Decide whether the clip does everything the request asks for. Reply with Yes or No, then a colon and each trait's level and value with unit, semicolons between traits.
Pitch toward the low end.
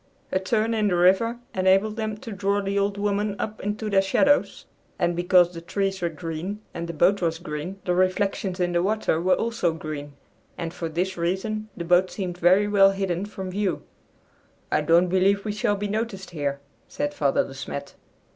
No: high, 190 Hz